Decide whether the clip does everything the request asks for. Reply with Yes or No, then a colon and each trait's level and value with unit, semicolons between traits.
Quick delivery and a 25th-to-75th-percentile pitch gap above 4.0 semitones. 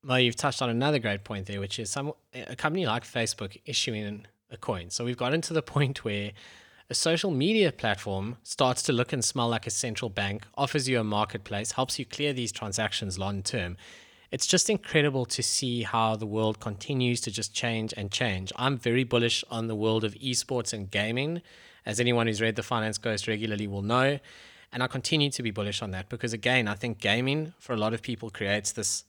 No: fast, 215 wpm; average, 3.4 semitones